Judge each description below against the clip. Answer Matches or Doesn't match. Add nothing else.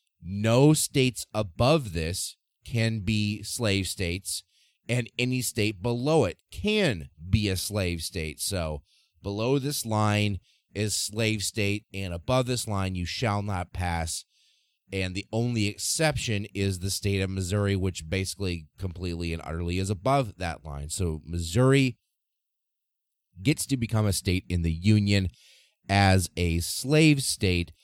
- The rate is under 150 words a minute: Matches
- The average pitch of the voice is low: Matches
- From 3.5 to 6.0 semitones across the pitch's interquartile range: Matches